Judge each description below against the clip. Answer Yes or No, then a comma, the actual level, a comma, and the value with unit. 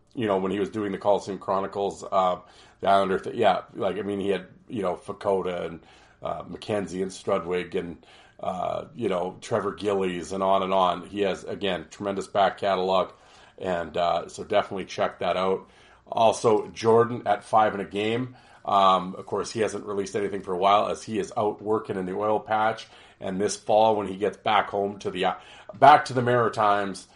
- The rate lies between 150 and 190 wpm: No, average, 200 wpm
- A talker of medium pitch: No, low, 100 Hz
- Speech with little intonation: Yes, narrow, 1.9 semitones